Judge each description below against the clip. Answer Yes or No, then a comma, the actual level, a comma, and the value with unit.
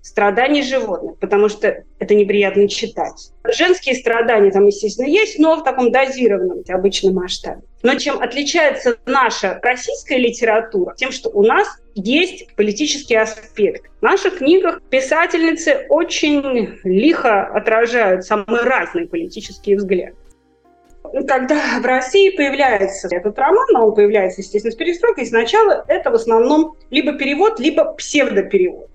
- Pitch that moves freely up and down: Yes, wide, 7.7 semitones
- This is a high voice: Yes, very high, 265 Hz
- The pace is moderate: Yes, average, 130 wpm